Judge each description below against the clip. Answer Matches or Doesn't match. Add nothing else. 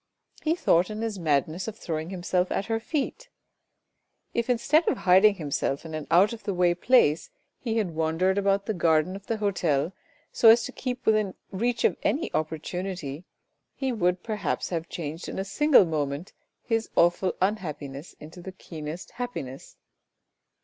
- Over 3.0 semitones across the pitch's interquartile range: Matches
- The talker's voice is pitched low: Doesn't match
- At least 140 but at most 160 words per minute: Doesn't match